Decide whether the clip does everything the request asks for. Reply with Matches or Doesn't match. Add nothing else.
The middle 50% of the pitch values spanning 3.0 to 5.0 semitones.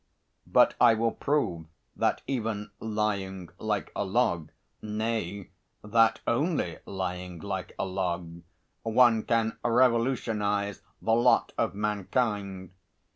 Matches